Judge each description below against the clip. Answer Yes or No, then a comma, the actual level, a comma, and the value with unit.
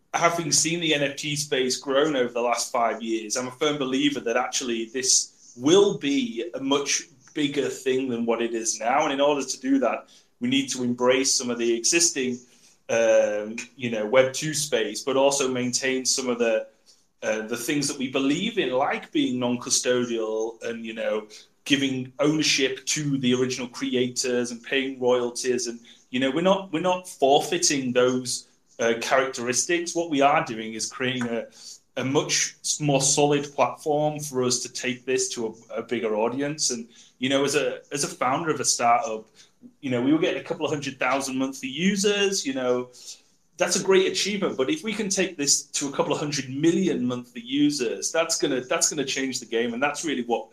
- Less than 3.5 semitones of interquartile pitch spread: No, average, 3.8 semitones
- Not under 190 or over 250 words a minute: Yes, average, 195 wpm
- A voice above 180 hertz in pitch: No, low, 135 Hz